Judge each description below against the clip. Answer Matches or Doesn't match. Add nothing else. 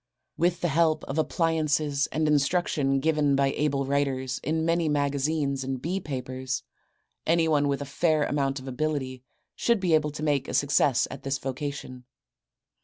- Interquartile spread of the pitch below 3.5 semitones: Matches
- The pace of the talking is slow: Doesn't match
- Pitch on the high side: Doesn't match